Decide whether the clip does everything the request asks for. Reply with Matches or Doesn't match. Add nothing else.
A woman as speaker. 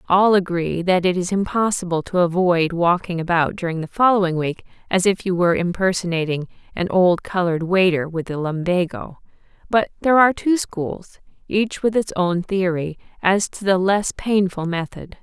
Matches